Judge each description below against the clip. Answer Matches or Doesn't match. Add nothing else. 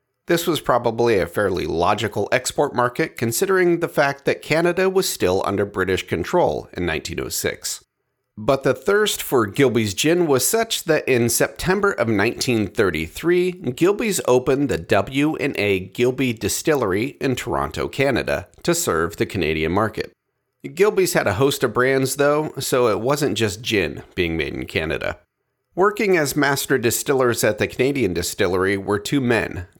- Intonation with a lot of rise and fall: Matches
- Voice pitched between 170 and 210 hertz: Doesn't match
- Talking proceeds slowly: Doesn't match